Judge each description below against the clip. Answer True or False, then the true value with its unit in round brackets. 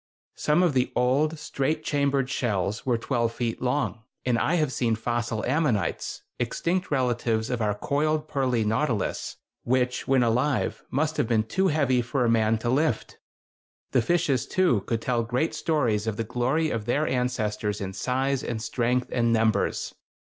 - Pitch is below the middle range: True (125 Hz)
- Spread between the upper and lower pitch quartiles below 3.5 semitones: False (3.9 semitones)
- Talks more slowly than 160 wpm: False (165 wpm)